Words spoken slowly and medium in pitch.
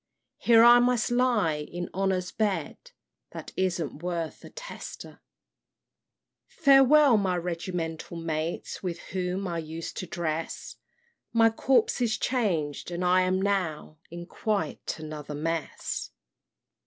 Yes: slow, 120 wpm; medium, 180 Hz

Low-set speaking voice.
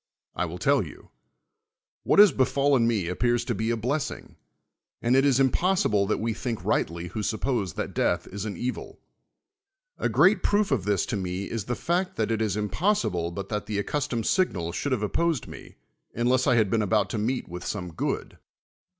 Yes: low, 115 Hz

